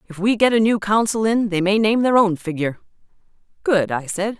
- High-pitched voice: Yes, high, 205 Hz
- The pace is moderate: No, fast, 220 wpm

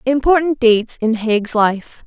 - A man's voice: No, female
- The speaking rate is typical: Yes, average, 145 wpm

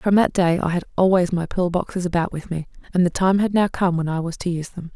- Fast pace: Yes, fast, 290 wpm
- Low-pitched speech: No, medium, 175 Hz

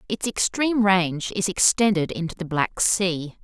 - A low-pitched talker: No, high, 190 Hz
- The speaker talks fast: No, average, 155 wpm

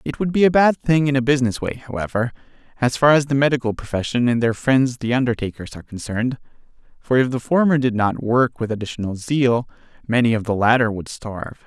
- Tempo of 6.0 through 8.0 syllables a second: Yes, 6.1 syllables/s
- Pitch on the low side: Yes, low, 125 Hz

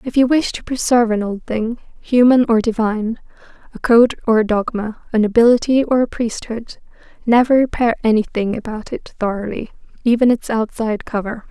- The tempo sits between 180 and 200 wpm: No, average, 160 wpm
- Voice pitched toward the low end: No, high, 230 Hz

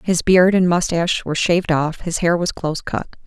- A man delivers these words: No, female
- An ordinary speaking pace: No, fast, 220 wpm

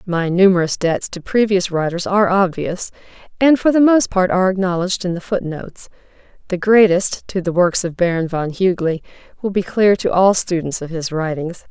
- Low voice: No, medium, 180 Hz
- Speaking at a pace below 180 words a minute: No, average, 185 wpm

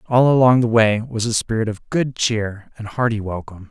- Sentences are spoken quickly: Yes, fast, 210 wpm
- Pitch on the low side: Yes, low, 115 Hz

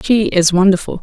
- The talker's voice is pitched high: Yes, high, 195 Hz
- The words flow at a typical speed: Yes, average, 175 wpm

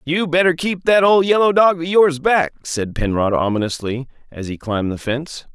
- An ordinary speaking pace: Yes, average, 195 wpm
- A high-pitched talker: No, medium, 150 Hz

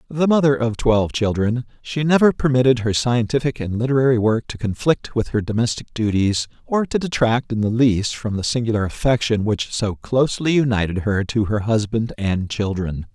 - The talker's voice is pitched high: No, low, 115 Hz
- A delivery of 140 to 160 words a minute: No, average, 180 wpm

